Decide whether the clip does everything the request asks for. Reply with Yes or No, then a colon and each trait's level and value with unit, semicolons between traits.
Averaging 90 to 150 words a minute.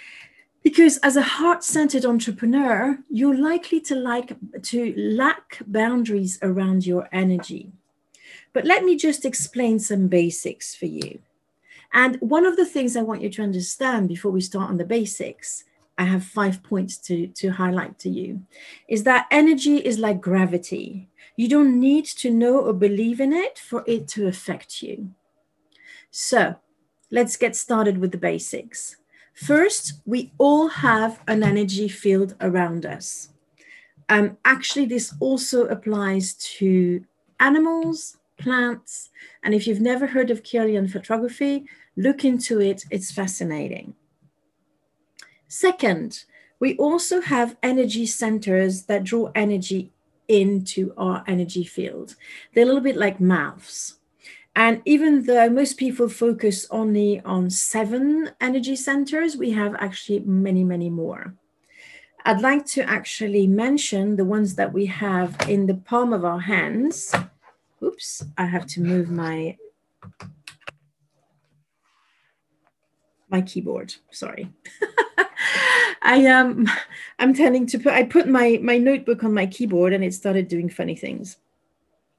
Yes: slow, 135 wpm